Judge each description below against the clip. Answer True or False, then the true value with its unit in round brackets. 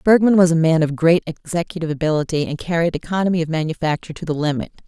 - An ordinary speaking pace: True (195 wpm)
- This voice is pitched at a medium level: True (165 Hz)